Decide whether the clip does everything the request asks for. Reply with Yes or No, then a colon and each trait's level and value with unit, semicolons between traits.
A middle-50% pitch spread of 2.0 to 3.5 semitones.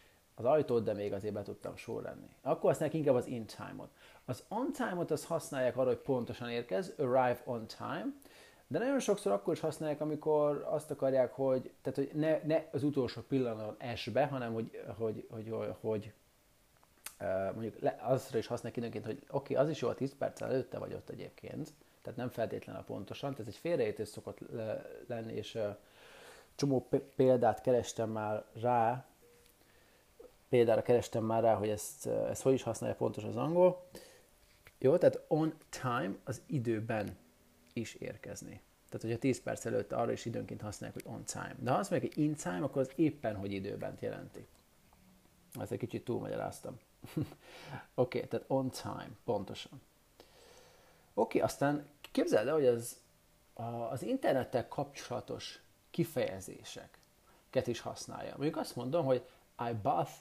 No: average, 4.8 semitones